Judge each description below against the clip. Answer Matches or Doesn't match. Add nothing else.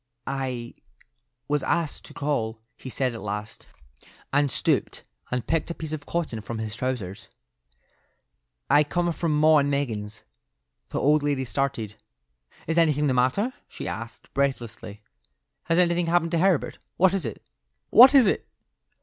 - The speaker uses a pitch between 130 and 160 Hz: Matches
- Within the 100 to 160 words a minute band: Matches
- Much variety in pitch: Matches